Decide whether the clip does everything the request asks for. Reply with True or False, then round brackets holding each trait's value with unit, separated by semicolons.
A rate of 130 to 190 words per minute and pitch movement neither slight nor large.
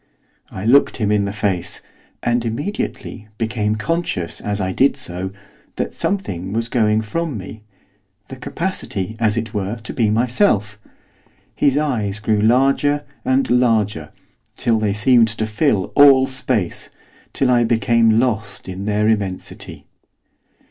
True (140 wpm; 3.7 semitones)